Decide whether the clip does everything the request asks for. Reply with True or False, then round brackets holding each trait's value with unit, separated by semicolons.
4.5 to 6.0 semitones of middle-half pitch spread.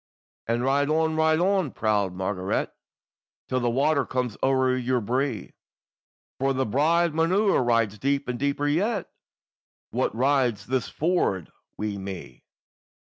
True (5.1 semitones)